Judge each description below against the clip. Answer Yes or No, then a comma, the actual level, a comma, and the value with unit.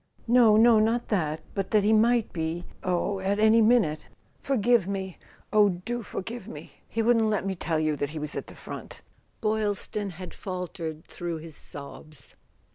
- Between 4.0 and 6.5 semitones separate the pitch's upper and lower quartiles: Yes, average, 4.7 semitones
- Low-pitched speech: No, high, 195 Hz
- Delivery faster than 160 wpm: Yes, average, 175 wpm